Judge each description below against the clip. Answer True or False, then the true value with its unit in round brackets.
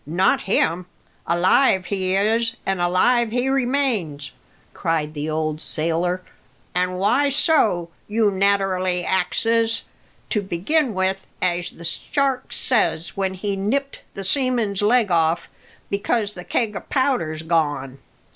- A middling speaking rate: False (125 wpm)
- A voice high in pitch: True (195 Hz)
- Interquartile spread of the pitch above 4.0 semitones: True (4.9 semitones)